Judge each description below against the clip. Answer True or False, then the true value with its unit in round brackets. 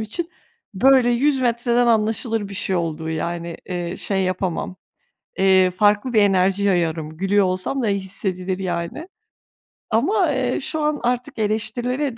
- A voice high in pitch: True (205 Hz)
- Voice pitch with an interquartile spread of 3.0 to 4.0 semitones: False (5.0 semitones)